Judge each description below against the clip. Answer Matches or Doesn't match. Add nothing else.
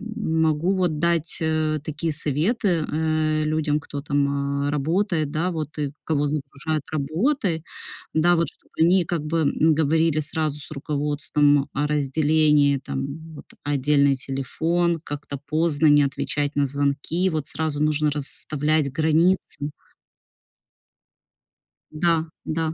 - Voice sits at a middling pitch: Matches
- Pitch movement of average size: Doesn't match